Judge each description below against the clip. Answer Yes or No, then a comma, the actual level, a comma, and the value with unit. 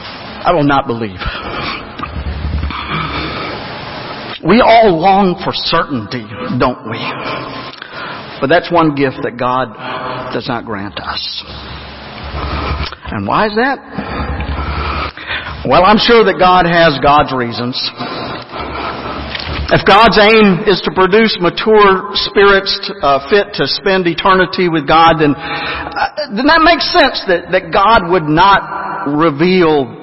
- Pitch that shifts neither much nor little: No, wide, 8.6 semitones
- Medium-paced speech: No, slow, 120 wpm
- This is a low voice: No, medium, 165 Hz